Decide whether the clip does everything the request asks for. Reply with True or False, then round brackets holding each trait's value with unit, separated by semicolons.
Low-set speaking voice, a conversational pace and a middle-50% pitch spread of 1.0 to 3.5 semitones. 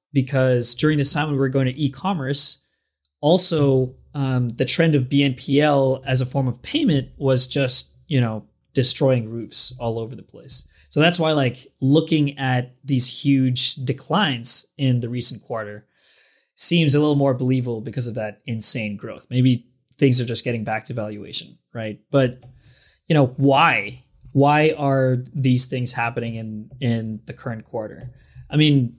True (130 Hz; 165 wpm; 2.8 semitones)